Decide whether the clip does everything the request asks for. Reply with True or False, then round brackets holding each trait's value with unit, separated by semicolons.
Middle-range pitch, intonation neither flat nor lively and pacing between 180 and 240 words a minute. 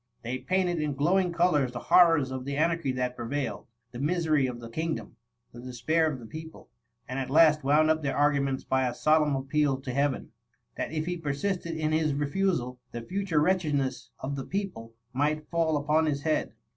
True (150 Hz; 3.6 semitones; 190 wpm)